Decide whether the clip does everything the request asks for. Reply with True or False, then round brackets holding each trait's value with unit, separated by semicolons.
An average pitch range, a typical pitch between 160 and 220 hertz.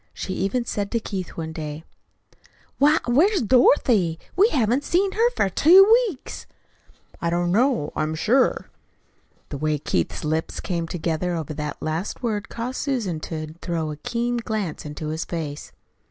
False (7.9 semitones; 185 Hz)